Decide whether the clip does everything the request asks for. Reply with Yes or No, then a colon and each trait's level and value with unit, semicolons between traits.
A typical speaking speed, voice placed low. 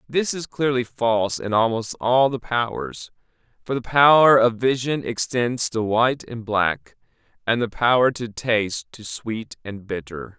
Yes: average, 160 wpm; low, 115 Hz